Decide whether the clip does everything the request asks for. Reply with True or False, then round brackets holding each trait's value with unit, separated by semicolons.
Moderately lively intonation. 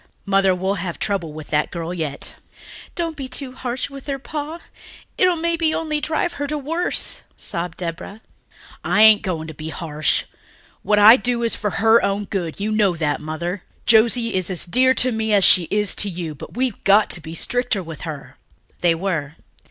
False (7.0 semitones)